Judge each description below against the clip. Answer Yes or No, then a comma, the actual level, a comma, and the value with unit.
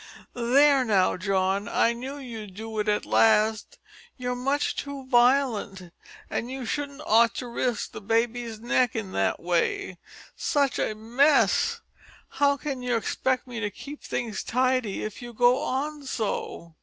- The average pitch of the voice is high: Yes, high, 240 Hz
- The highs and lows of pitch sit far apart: No, average, 3.7 semitones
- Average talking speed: Yes, average, 155 wpm